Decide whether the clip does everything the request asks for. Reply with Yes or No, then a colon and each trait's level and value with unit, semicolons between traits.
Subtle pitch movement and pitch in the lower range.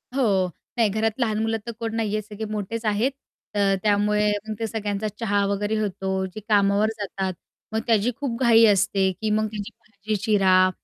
No: narrow, 1.8 semitones; high, 210 Hz